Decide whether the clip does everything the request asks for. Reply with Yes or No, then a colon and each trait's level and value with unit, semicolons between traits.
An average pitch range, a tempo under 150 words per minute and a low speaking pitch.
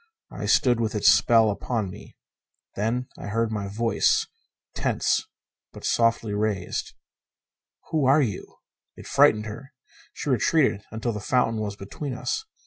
Yes: average, 3.1 semitones; average, 140 wpm; low, 115 Hz